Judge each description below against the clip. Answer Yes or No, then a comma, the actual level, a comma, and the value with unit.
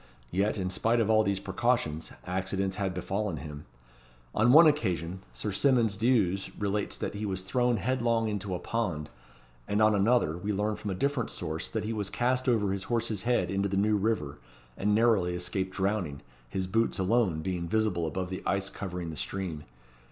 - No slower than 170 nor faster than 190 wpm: Yes, average, 185 wpm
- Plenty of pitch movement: No, average, 3.4 semitones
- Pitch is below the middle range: Yes, low, 100 Hz